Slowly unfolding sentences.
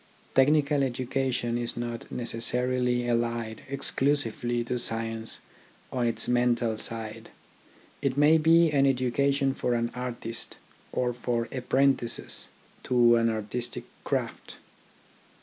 Yes: slow, 110 wpm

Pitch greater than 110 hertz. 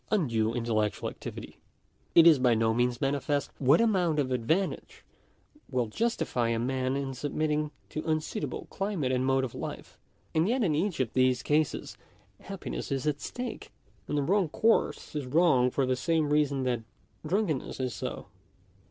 Yes: medium, 140 Hz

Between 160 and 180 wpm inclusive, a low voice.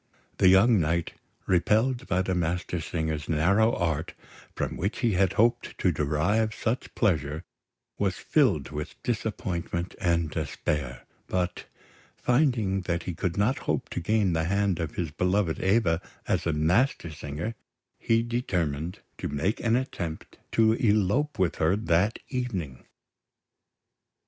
No: slow, 135 wpm; very low, 90 Hz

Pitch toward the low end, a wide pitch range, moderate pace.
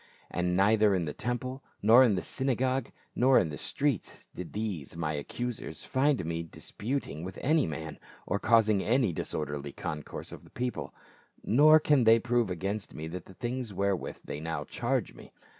Yes: low, 105 Hz; wide, 6.9 semitones; average, 165 wpm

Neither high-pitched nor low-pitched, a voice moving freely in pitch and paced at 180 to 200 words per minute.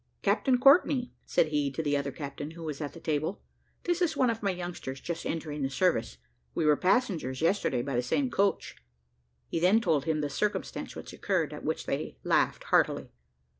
Yes: medium, 160 Hz; wide, 6.1 semitones; average, 195 wpm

